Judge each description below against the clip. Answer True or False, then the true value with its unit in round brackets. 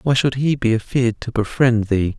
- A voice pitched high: False (120 Hz)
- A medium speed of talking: False (220 wpm)